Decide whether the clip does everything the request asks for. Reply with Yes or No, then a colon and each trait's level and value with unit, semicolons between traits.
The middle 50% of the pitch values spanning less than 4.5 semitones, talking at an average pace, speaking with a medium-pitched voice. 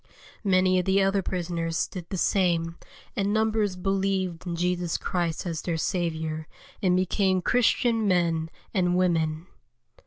Yes: narrow, 2.5 semitones; average, 145 wpm; medium, 180 Hz